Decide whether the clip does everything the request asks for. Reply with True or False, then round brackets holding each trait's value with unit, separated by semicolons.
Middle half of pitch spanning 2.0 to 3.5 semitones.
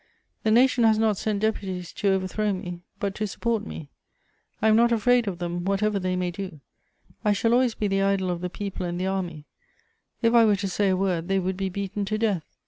True (2.8 semitones)